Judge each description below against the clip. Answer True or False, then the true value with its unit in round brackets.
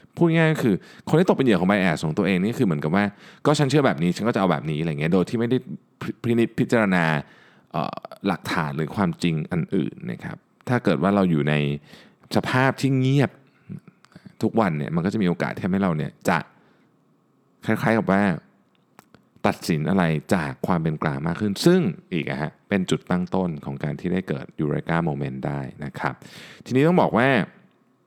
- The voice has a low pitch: True (100 Hz)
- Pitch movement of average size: False (8.2 semitones)